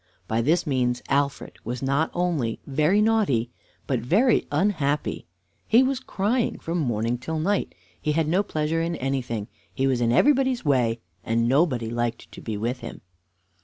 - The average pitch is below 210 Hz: Yes, medium, 140 Hz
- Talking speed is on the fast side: No, average, 165 wpm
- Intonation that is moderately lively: No, wide, 6.6 semitones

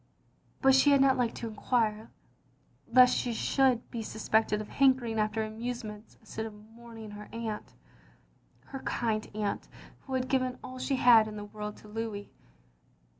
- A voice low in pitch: No, high, 225 Hz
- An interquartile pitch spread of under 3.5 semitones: Yes, average, 2.9 semitones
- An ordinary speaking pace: Yes, average, 160 wpm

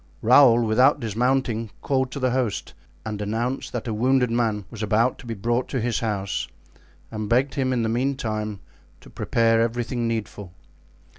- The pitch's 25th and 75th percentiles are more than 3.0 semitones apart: No, narrow, 2.6 semitones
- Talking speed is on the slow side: No, average, 165 wpm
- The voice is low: Yes, low, 115 Hz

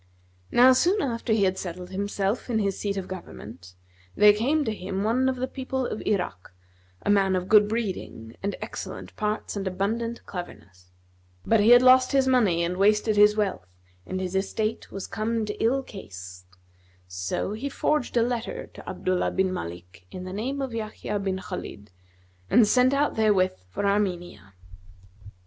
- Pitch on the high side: Yes, high, 205 Hz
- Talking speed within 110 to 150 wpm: No, average, 170 wpm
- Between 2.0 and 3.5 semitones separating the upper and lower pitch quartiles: No, average, 4.1 semitones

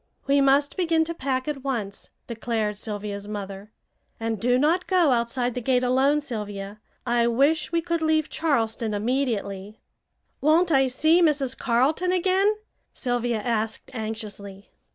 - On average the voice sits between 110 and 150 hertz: No, very high, 250 Hz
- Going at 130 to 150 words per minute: Yes, average, 140 wpm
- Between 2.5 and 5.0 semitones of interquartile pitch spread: No, wide, 5.5 semitones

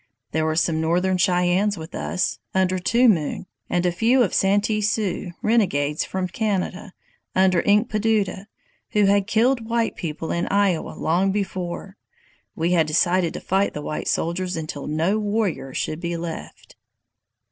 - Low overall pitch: No, medium, 185 Hz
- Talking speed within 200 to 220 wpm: No, average, 145 wpm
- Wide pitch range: No, average, 3.3 semitones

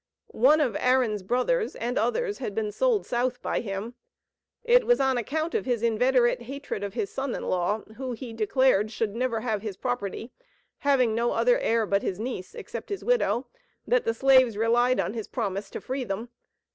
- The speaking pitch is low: No, high, 245 Hz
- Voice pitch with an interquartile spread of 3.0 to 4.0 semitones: Yes, average, 3.7 semitones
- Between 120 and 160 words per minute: No, average, 190 wpm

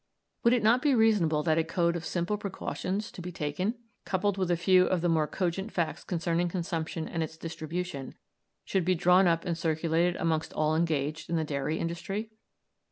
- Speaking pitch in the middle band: Yes, medium, 170 Hz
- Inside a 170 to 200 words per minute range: Yes, average, 190 wpm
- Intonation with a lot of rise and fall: No, narrow, 2.6 semitones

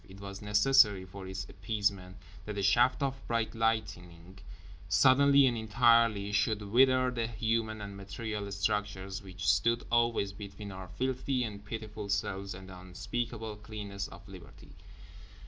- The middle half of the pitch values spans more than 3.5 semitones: No, average, 2.9 semitones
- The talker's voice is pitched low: Yes, low, 105 Hz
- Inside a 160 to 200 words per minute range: No, average, 145 wpm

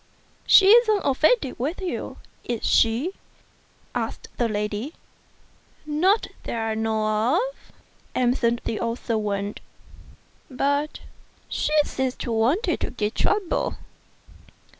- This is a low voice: No, very high, 250 Hz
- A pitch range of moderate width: No, wide, 6.9 semitones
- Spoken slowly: Yes, slow, 115 wpm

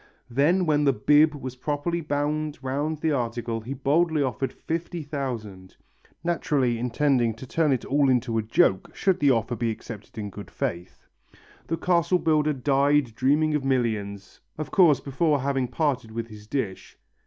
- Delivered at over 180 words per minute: No, average, 165 wpm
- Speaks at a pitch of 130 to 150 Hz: Yes, low, 135 Hz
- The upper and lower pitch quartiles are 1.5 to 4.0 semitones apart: No, average, 4.5 semitones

